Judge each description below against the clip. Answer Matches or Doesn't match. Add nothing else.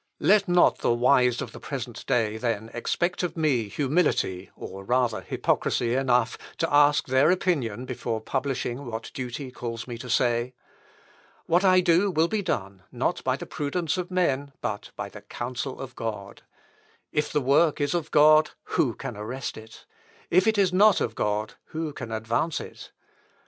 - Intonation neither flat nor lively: Doesn't match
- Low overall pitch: Matches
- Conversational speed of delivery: Matches